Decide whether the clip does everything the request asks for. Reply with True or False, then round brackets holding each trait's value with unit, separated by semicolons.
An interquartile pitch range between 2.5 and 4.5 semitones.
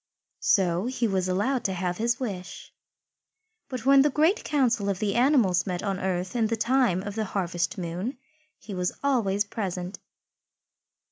False (5.2 semitones)